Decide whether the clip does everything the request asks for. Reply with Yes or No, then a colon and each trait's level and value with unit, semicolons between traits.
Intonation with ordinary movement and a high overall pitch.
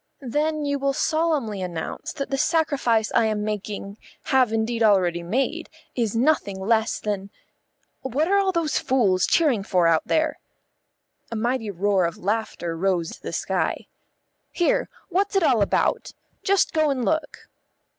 No: wide, 7.1 semitones; high, 230 Hz